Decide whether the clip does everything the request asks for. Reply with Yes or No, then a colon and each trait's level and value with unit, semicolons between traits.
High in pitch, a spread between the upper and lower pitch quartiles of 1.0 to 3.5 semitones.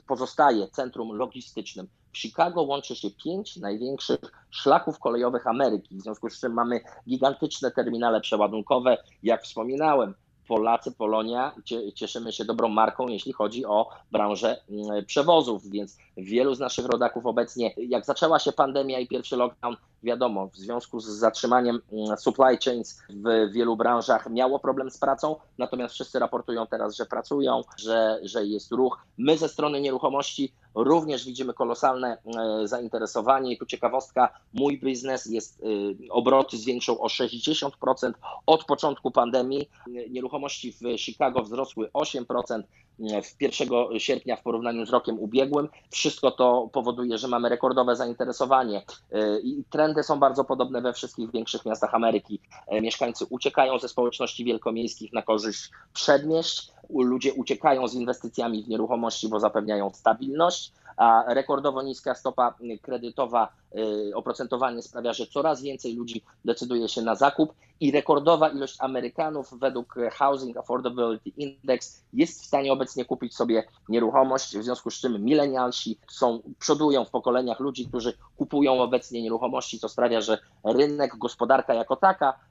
No: low, 125 Hz; average, 2.9 semitones